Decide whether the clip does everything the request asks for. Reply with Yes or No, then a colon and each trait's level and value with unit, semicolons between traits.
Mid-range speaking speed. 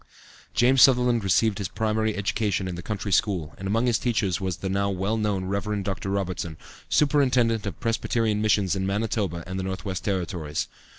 Yes: average, 180 wpm